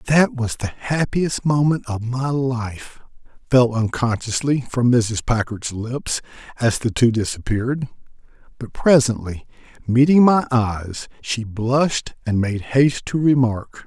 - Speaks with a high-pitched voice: No, low, 120 Hz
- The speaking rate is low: Yes, slow, 130 wpm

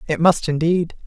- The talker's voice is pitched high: No, medium, 165 Hz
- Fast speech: No, average, 170 wpm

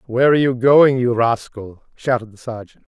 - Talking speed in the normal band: Yes, average, 185 wpm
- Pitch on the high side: No, low, 120 Hz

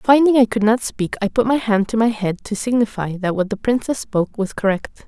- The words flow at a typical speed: No, fast, 250 wpm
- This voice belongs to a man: No, female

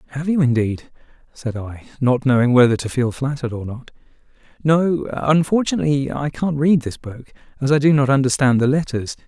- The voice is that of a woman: No, male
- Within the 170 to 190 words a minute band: Yes, average, 175 wpm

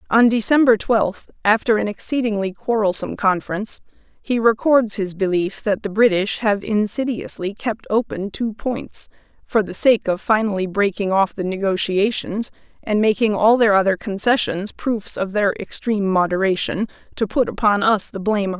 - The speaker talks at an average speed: Yes, average, 160 wpm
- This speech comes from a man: No, female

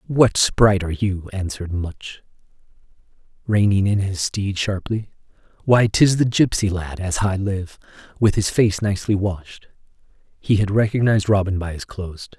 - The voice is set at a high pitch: No, low, 100 Hz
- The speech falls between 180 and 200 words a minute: No, average, 150 wpm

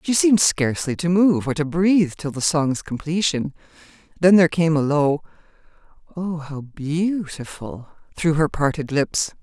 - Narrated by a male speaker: No, female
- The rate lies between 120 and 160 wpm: Yes, average, 155 wpm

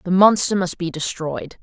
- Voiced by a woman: Yes, female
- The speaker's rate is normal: Yes, average, 185 wpm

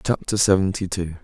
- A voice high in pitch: No, very low, 95 Hz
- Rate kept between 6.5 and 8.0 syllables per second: No, 5.6 syllables/s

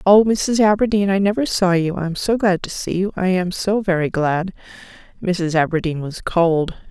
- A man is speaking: No, female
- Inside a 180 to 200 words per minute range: Yes, average, 190 wpm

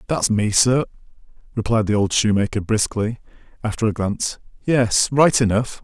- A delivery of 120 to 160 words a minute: Yes, slow, 135 wpm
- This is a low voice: Yes, low, 110 Hz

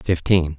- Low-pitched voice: Yes, very low, 85 Hz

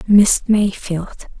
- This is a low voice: No, high, 200 Hz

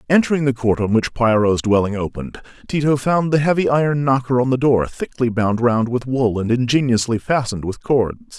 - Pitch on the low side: Yes, low, 125 Hz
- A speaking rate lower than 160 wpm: No, average, 195 wpm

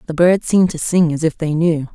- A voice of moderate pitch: Yes, medium, 165 Hz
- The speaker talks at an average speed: No, fast, 280 wpm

